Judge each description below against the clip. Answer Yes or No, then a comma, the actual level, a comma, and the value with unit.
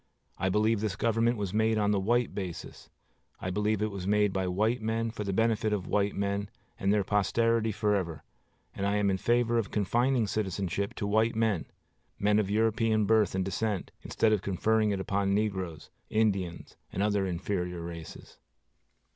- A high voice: No, low, 105 Hz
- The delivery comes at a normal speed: Yes, average, 175 wpm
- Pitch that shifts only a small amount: Yes, narrow, 2.3 semitones